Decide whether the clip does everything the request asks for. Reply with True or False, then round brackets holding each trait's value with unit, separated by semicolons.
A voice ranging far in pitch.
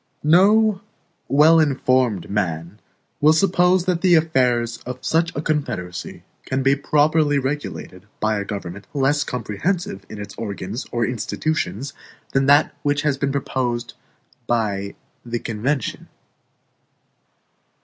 True (6.0 semitones)